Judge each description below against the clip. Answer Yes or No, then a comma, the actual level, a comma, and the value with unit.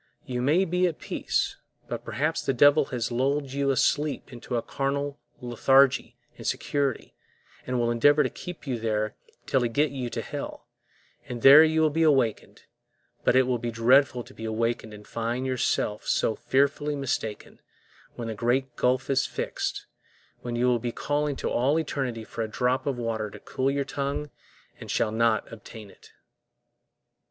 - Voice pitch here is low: Yes, low, 130 Hz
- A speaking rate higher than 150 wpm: Yes, average, 180 wpm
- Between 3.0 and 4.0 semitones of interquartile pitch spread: Yes, average, 3.3 semitones